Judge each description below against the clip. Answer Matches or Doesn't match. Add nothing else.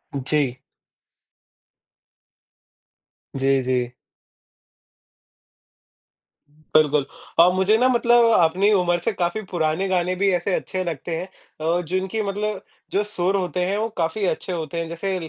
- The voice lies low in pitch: Doesn't match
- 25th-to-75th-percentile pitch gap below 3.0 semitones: Doesn't match